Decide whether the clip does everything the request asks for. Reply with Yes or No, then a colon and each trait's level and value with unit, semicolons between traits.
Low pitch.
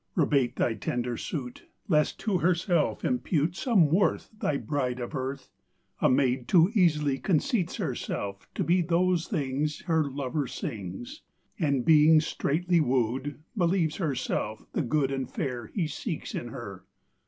No: medium, 150 Hz